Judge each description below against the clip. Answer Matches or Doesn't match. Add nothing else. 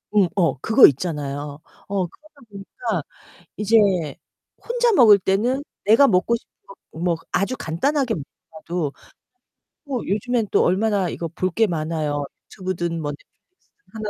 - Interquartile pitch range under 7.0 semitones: Matches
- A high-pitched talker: Matches